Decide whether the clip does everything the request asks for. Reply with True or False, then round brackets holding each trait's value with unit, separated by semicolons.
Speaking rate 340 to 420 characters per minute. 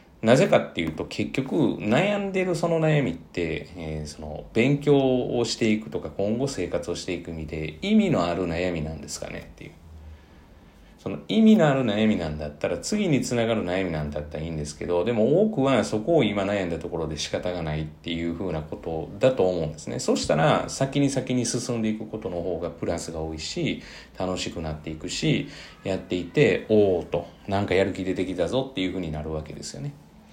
True (355 characters per minute)